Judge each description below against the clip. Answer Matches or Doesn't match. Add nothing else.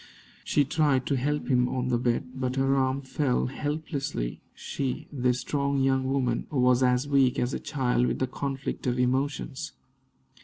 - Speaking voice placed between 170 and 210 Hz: Doesn't match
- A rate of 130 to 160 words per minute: Doesn't match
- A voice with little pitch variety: Matches